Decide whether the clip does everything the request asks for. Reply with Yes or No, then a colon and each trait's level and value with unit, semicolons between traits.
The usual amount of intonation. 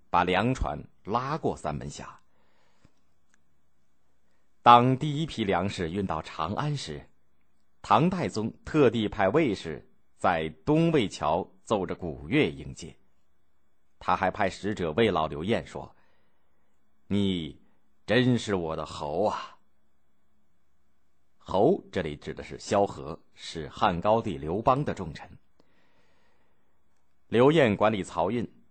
No: wide, 5.9 semitones